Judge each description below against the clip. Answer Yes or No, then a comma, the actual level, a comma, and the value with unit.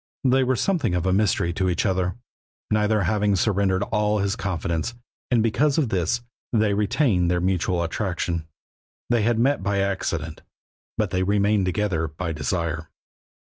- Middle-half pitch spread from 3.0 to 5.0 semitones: Yes, average, 3.4 semitones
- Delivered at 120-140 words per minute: No, average, 155 wpm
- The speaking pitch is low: Yes, low, 100 Hz